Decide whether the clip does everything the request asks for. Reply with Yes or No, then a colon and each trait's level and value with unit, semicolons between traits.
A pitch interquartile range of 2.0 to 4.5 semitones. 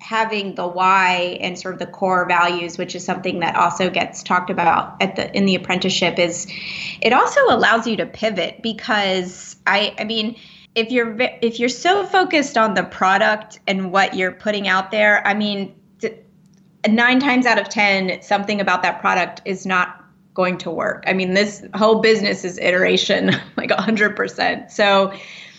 Yes: average, 3.1 semitones